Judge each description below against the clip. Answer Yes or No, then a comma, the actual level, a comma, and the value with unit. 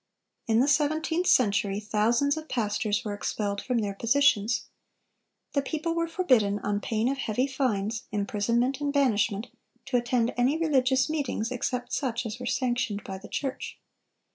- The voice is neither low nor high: No, high, 245 Hz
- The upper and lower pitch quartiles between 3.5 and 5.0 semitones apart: Yes, average, 4.7 semitones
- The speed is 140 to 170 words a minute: Yes, average, 155 wpm